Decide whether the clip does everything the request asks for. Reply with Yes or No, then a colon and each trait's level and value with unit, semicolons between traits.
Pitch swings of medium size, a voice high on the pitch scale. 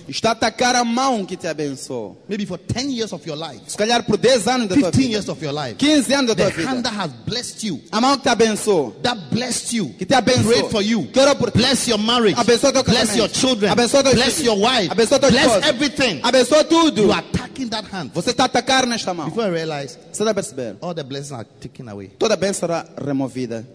No: wide, 6.6 semitones; high, 220 Hz